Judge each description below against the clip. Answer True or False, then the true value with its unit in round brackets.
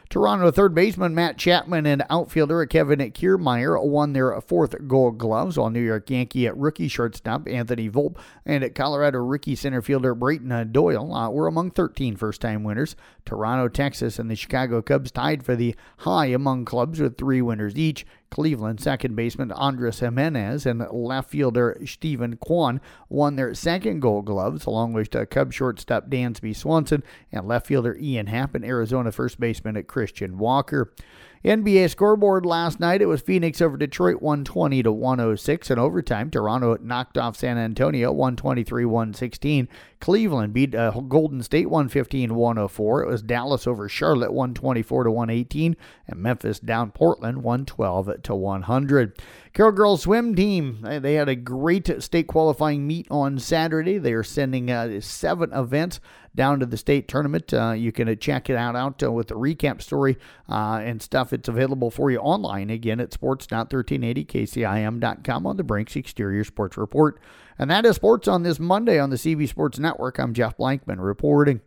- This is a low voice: True (130 Hz)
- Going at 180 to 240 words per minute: False (165 wpm)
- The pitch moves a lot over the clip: False (4.3 semitones)